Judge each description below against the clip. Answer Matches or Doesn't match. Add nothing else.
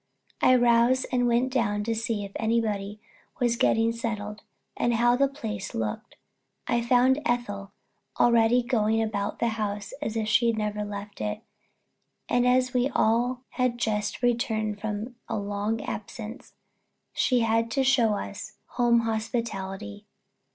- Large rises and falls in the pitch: Doesn't match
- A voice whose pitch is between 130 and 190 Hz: Doesn't match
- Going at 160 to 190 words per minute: Doesn't match